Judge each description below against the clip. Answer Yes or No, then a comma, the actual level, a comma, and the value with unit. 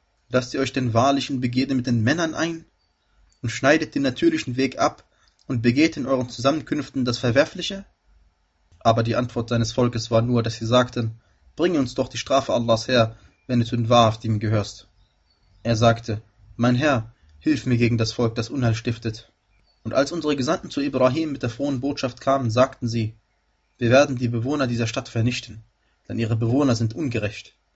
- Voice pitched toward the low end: Yes, low, 120 Hz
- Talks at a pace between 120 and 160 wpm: No, average, 180 wpm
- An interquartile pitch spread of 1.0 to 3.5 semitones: Yes, average, 3.0 semitones